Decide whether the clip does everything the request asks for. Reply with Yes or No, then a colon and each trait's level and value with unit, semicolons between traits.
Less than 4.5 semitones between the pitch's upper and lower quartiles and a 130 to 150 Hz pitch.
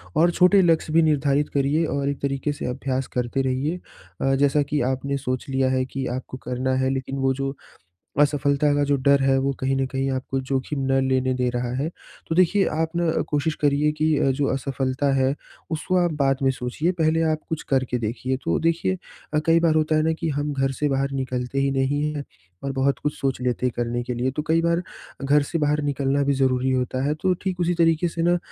Yes: average, 2.7 semitones; medium, 140 Hz